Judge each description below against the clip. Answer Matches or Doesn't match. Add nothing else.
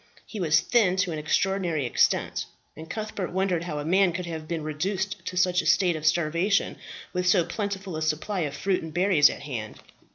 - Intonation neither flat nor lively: Matches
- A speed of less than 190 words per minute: Doesn't match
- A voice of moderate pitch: Matches